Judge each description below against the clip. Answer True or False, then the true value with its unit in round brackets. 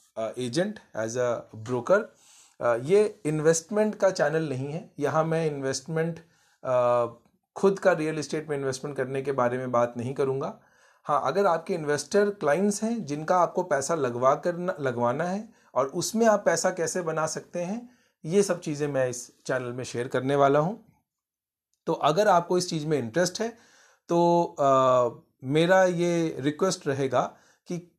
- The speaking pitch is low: False (160 Hz)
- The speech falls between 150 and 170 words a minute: True (160 wpm)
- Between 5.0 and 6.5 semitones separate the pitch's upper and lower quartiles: True (5.6 semitones)